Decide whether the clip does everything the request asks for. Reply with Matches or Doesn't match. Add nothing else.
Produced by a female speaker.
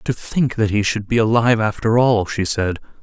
Doesn't match